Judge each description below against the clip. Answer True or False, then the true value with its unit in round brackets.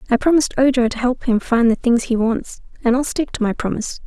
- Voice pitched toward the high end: True (240 Hz)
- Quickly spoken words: True (250 wpm)